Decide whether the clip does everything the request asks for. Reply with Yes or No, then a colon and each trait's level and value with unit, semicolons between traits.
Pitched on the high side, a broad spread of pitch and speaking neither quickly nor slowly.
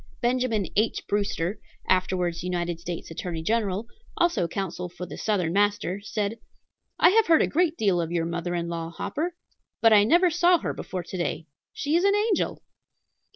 Yes: high, 200 Hz; wide, 6.6 semitones; average, 175 wpm